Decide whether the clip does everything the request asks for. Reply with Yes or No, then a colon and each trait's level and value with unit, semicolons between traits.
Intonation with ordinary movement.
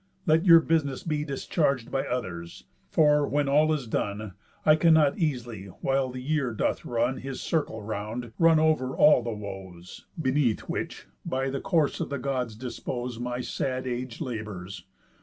Yes: average, 4.5 semitones